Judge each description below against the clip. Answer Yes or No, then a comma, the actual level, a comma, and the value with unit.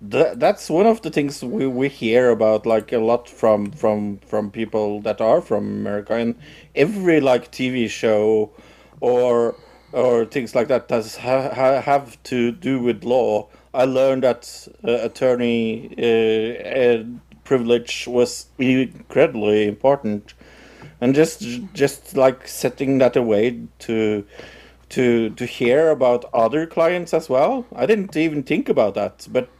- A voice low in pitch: Yes, low, 125 Hz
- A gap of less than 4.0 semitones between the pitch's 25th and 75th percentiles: Yes, average, 3.4 semitones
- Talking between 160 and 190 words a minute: No, average, 150 wpm